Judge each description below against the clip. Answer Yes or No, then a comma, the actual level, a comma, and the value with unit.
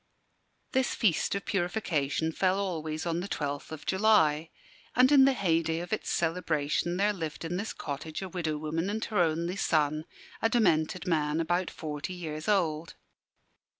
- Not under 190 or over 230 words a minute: No, average, 160 wpm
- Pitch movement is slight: No, average, 3.7 semitones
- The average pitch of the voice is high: No, medium, 170 Hz